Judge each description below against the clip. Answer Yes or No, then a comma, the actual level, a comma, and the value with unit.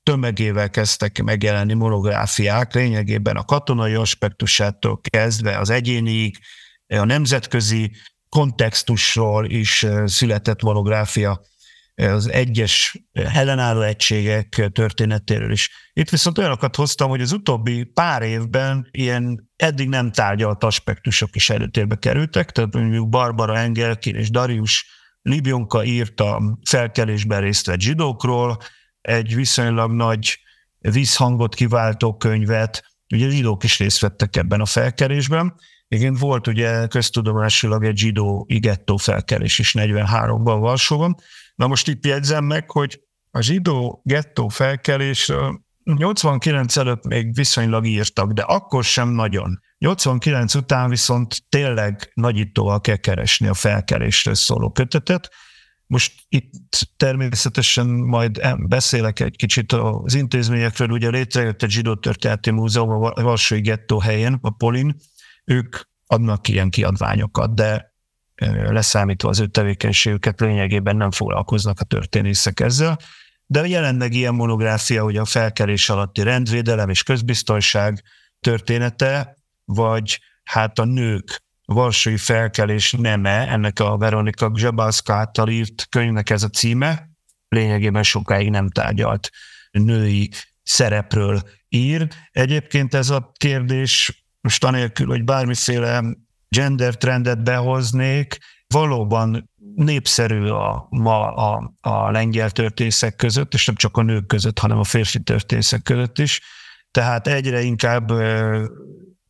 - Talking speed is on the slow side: No, average, 120 wpm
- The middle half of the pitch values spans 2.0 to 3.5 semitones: Yes, average, 3.1 semitones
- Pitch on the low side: Yes, low, 115 Hz